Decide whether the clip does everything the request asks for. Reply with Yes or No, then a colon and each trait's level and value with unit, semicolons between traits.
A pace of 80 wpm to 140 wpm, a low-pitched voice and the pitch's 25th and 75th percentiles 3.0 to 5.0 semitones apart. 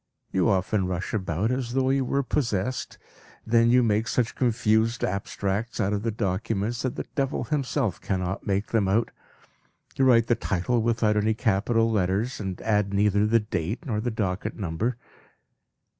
No: average, 160 wpm; low, 110 Hz; average, 3.3 semitones